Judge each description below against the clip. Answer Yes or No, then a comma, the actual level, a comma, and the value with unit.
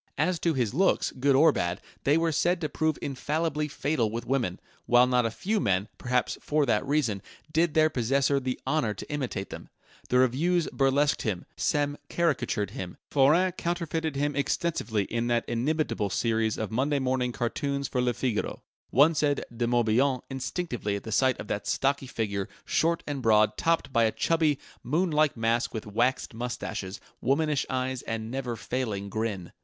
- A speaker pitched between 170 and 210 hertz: No, low, 130 Hz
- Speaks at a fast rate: No, average, 170 wpm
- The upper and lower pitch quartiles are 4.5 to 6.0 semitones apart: Yes, average, 4.8 semitones